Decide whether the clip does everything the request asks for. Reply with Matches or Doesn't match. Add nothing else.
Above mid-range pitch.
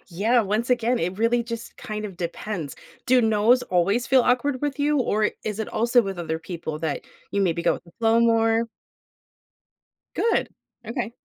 Matches